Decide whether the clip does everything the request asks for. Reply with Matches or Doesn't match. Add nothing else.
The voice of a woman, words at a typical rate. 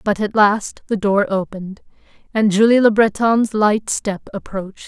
Matches